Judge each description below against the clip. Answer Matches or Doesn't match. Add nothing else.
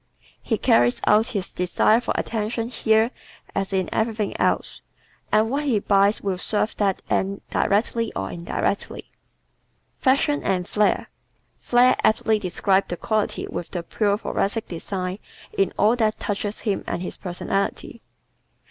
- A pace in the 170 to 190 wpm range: Doesn't match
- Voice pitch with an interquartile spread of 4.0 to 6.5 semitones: Doesn't match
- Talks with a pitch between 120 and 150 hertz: Doesn't match